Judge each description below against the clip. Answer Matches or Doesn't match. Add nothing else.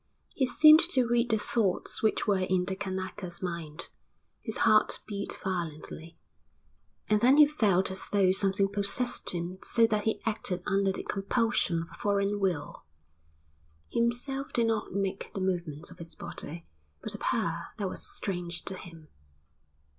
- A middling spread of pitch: Matches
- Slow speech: Doesn't match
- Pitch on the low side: Doesn't match